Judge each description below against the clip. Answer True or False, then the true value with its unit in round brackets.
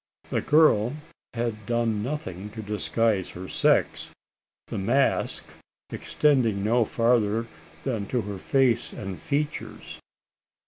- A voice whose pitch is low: True (115 Hz)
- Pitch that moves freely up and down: False (3.3 semitones)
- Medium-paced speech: False (110 wpm)